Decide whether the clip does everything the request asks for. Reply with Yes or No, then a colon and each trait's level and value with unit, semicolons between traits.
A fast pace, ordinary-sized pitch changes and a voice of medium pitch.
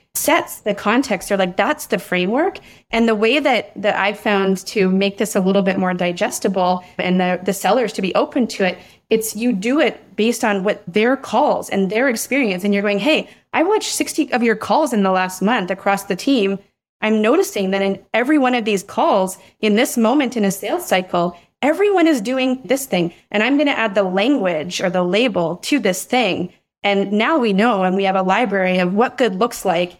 No: fast, 220 wpm; average, 4.3 semitones; high, 210 Hz